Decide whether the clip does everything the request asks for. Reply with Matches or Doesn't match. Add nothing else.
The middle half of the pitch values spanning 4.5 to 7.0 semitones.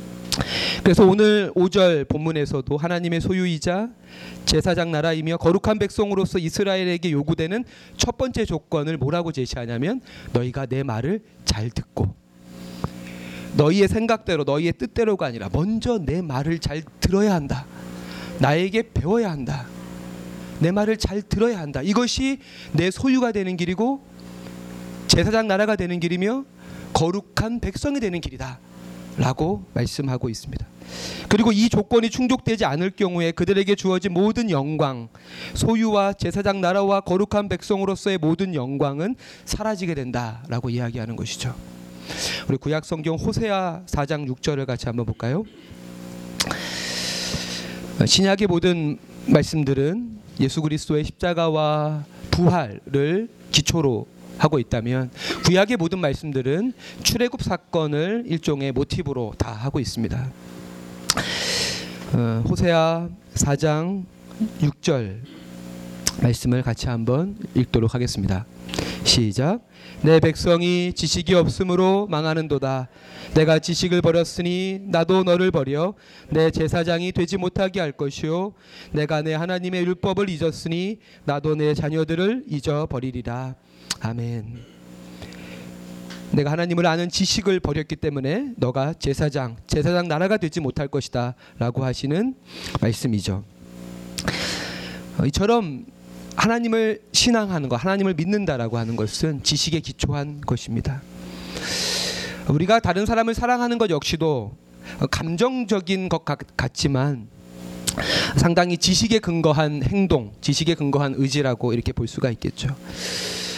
Doesn't match